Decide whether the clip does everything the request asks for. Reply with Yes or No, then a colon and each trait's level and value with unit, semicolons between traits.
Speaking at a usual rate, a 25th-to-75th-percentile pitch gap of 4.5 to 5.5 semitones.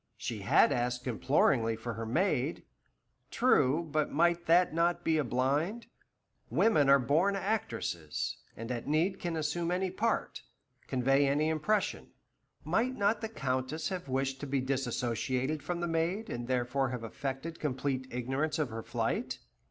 Yes: average, 150 wpm; average, 5.2 semitones